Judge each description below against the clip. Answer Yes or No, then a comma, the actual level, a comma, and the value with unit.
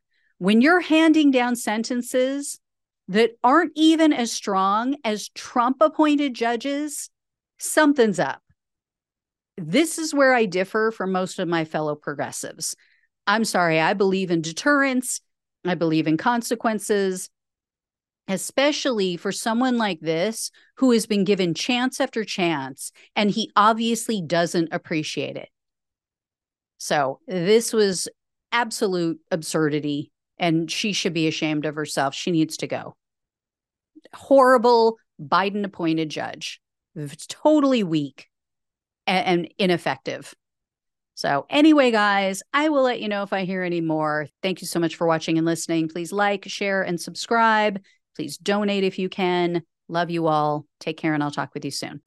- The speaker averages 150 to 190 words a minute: No, average, 140 wpm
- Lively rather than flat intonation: Yes, wide, 6.3 semitones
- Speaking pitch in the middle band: No, high, 195 Hz